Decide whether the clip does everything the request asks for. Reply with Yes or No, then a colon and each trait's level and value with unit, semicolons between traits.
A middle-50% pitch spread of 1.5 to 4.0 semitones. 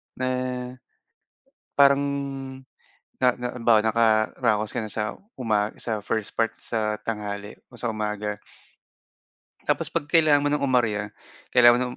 Yes: average, 2.8 semitones